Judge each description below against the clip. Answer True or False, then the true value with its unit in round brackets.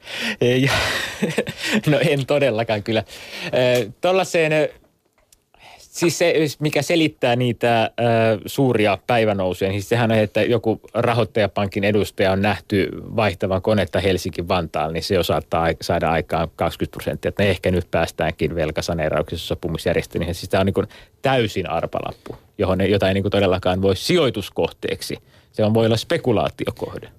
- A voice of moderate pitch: False (105 Hz)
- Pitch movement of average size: True (4.5 semitones)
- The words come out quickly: False (130 wpm)